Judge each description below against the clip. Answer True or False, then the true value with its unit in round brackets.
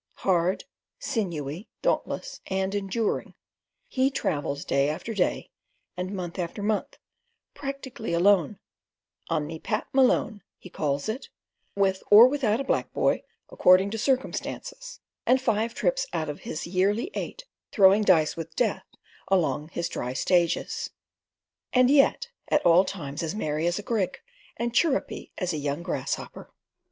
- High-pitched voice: True (195 Hz)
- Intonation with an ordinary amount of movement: False (5.8 semitones)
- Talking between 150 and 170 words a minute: False (140 wpm)